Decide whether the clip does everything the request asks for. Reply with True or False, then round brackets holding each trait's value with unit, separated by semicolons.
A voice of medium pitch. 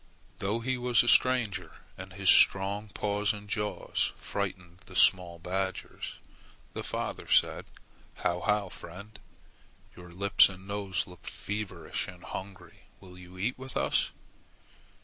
False (95 Hz)